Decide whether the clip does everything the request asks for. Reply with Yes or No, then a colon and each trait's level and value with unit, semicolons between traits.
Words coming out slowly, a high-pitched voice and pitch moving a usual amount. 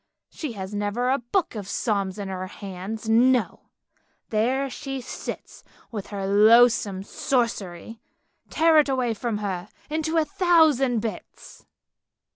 Yes: slow, 130 wpm; high, 230 Hz; average, 4.7 semitones